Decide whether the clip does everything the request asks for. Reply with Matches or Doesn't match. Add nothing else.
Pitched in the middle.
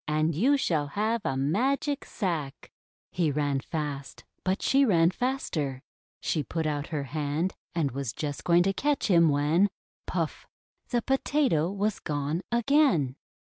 Matches